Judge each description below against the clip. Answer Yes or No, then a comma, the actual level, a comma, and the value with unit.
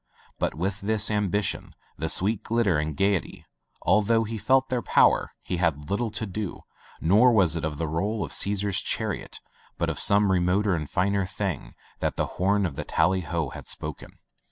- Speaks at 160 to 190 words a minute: Yes, average, 185 wpm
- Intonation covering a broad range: No, average, 3.5 semitones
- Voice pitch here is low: Yes, low, 100 Hz